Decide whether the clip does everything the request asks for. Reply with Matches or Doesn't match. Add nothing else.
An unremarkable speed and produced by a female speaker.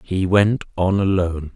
Doesn't match